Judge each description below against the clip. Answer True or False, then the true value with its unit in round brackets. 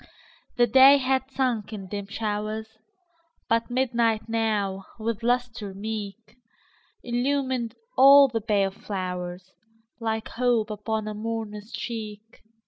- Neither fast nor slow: False (100 wpm)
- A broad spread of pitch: False (2.7 semitones)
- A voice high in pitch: True (225 Hz)